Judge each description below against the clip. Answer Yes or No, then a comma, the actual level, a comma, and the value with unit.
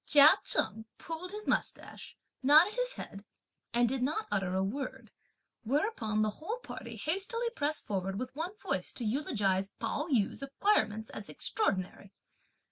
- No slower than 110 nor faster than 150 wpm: Yes, average, 145 wpm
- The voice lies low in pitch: No, very high, 270 Hz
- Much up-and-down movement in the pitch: Yes, wide, 8.5 semitones